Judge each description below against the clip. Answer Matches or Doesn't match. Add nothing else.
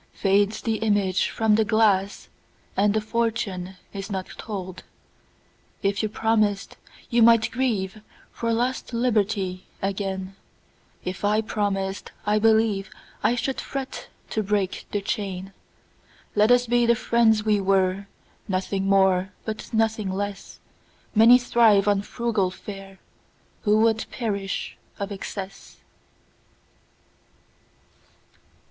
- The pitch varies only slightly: Matches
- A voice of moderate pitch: Doesn't match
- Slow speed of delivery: Matches